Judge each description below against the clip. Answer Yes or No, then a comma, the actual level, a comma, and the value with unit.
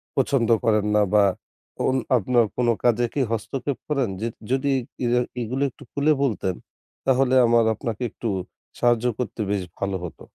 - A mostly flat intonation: No, average, 3.1 semitones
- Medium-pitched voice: No, low, 120 Hz